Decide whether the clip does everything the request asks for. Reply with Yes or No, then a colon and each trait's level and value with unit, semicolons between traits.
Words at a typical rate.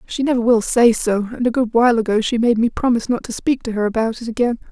No: fast, 280 wpm